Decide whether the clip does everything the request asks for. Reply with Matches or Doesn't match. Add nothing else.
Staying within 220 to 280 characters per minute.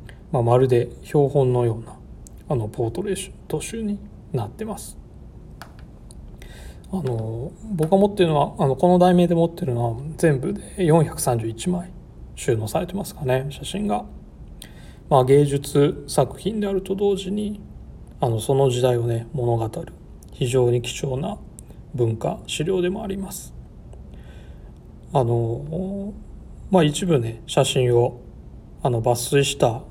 Matches